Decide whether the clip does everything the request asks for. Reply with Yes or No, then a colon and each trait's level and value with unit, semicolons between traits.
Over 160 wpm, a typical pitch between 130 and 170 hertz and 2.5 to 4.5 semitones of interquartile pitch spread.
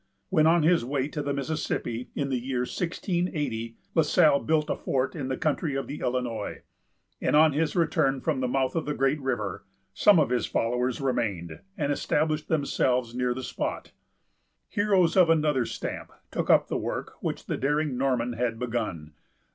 Yes: average, 180 wpm; low, 135 Hz; average, 3.9 semitones